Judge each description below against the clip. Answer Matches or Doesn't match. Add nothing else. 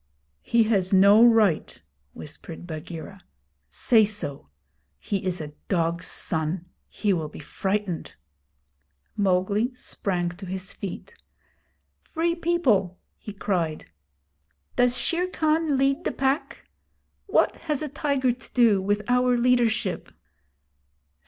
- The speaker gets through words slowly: Matches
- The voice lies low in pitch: Doesn't match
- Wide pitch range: Matches